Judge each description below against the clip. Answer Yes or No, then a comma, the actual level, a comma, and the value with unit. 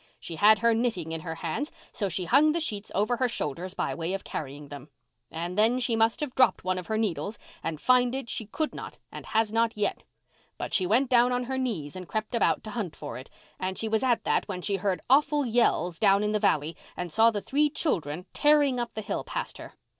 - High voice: Yes, high, 215 Hz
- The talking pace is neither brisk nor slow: No, fast, 235 wpm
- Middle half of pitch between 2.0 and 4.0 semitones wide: No, wide, 5.4 semitones